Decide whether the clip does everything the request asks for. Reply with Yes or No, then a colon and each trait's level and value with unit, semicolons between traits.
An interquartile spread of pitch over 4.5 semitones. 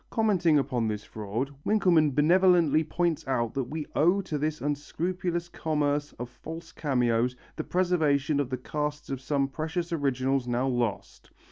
No: average, 4.2 semitones